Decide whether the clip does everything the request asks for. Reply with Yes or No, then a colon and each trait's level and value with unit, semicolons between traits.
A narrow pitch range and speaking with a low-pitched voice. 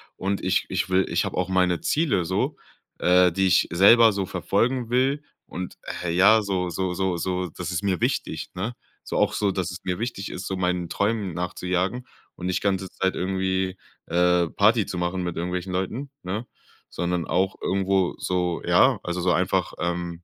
Yes: narrow, 1.7 semitones; very low, 95 Hz